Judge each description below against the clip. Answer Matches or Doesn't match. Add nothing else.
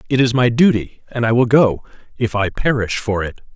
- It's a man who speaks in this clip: Matches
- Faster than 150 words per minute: Matches